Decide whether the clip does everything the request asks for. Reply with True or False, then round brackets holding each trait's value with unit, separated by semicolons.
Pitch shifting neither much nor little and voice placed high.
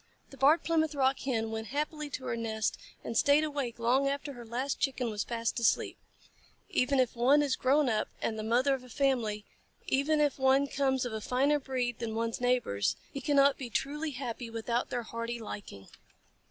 True (3.3 semitones; 255 Hz)